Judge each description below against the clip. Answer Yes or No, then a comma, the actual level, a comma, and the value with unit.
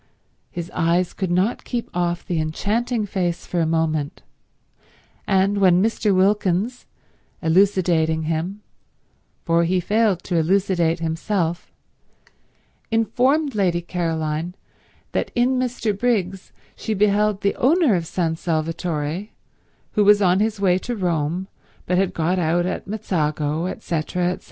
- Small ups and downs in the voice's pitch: No, average, 3.8 semitones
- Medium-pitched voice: Yes, medium, 180 Hz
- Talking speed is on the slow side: Yes, slow, 130 wpm